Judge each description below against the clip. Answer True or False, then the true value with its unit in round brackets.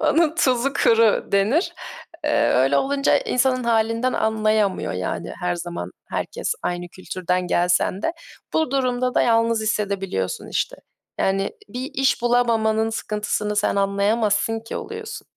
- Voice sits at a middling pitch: False (220 Hz)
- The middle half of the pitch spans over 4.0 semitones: True (4.4 semitones)